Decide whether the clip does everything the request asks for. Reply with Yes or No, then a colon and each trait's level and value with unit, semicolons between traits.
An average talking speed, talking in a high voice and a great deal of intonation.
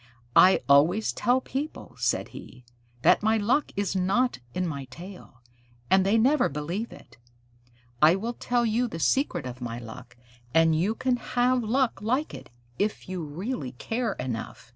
Yes: average, 165 wpm; high, 195 Hz; wide, 8.2 semitones